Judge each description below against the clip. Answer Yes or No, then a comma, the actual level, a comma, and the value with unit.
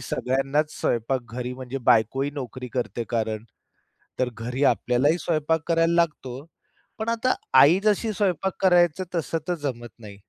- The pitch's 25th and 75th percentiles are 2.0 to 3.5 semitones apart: No, wide, 5.5 semitones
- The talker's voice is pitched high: No, medium, 140 Hz